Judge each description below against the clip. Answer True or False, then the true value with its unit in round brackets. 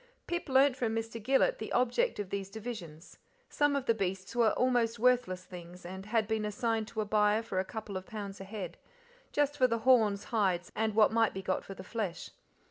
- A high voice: True (220 Hz)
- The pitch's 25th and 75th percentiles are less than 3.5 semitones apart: False (3.8 semitones)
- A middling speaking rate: False (210 wpm)